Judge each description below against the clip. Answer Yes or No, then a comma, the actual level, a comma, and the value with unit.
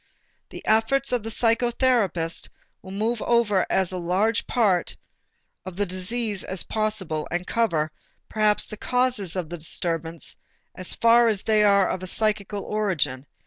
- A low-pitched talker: No, high, 205 Hz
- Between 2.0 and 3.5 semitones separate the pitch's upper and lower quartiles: No, average, 3.9 semitones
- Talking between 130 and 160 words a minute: Yes, average, 145 wpm